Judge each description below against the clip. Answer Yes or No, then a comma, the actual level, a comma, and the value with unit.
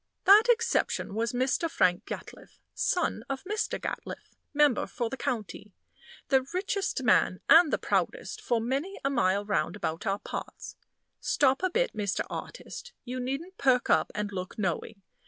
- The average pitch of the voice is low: No, very high, 255 Hz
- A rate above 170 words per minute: No, average, 155 wpm